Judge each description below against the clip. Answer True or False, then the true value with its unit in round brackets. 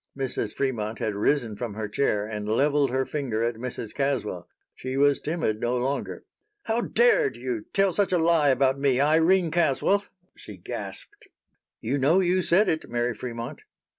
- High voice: False (135 Hz)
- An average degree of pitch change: False (6.3 semitones)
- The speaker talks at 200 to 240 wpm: False (165 wpm)